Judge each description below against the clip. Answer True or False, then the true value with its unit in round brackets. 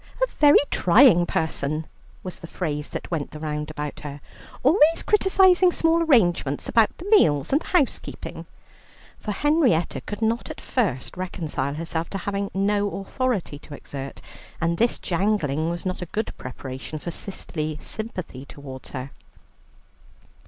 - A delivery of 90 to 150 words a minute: True (145 wpm)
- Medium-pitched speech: True (175 Hz)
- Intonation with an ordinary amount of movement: False (7.7 semitones)